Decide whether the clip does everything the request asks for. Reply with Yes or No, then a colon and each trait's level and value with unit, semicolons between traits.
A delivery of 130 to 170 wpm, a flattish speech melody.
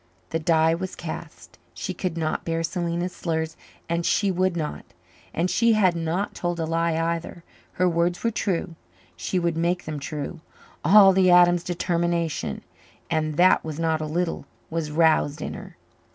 Yes: average, 165 wpm; narrow, 1.7 semitones